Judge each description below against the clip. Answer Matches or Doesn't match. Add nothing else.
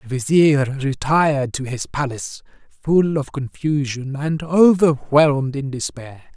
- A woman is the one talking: Doesn't match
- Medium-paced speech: Doesn't match